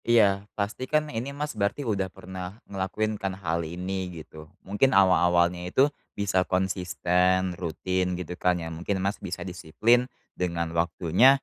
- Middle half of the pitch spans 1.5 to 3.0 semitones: Yes, average, 2.7 semitones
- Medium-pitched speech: No, very low, 95 Hz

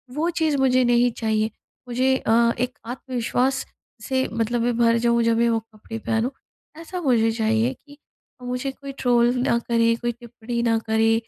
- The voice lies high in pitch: Yes, high, 240 Hz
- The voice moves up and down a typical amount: No, narrow, 2.0 semitones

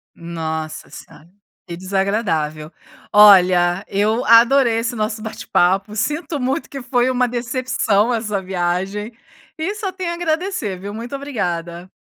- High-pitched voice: Yes, high, 215 Hz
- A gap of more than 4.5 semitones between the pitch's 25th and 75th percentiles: Yes, wide, 5.5 semitones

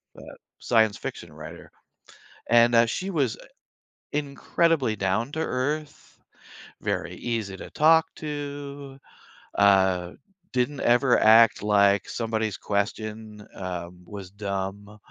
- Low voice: Yes, low, 110 Hz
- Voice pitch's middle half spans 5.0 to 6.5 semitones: Yes, wide, 5.6 semitones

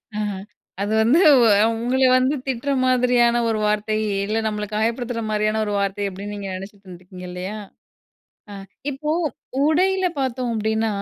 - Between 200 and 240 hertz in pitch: Yes, high, 220 Hz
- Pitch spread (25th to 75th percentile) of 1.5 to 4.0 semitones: Yes, average, 3.4 semitones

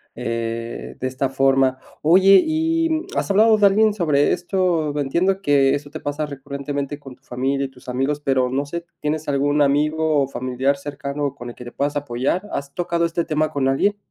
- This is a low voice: No, medium, 145 Hz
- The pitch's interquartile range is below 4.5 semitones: Yes, average, 3.9 semitones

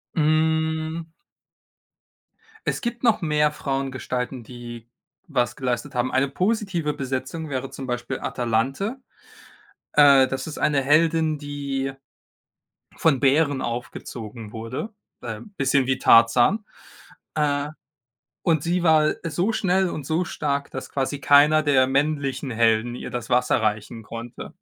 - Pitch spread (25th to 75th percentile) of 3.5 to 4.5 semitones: Yes, average, 4.0 semitones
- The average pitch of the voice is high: No, medium, 140 Hz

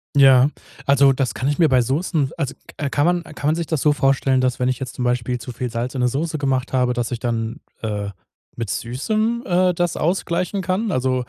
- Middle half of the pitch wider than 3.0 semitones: Yes, average, 4.5 semitones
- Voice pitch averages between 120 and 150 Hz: Yes, low, 135 Hz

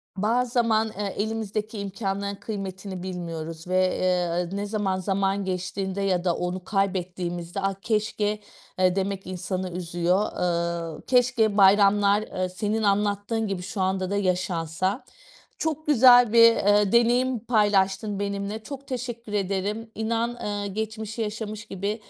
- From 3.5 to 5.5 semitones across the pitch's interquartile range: No, average, 2.9 semitones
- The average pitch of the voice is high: Yes, high, 200 Hz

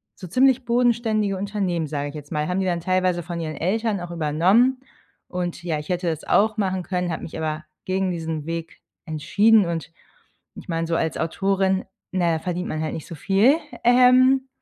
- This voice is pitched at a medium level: Yes, medium, 180 Hz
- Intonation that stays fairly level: No, average, 4.1 semitones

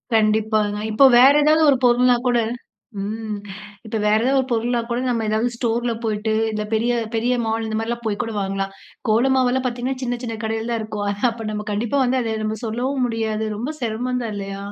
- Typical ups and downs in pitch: No, narrow, 2.1 semitones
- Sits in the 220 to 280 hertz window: Yes, high, 225 Hz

